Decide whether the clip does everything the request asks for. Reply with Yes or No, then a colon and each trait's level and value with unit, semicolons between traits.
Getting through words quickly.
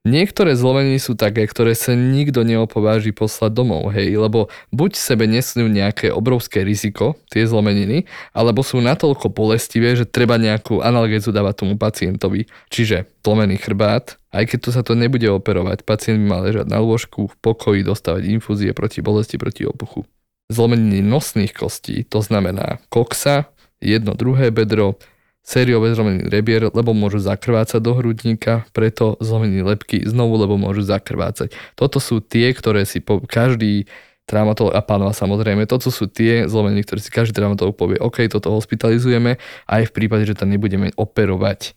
No: average, 155 wpm